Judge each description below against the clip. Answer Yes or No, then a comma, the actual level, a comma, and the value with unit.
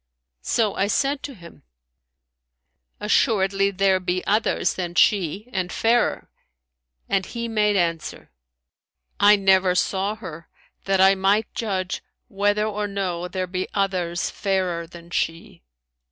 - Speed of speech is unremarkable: No, slow, 125 wpm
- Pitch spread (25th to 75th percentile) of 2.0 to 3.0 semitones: Yes, narrow, 2.4 semitones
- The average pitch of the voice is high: Yes, high, 195 Hz